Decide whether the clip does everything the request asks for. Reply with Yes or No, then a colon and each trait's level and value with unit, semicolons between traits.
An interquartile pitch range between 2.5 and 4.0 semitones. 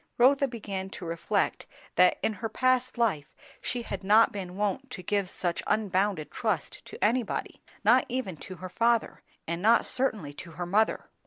No: average, 4.4 semitones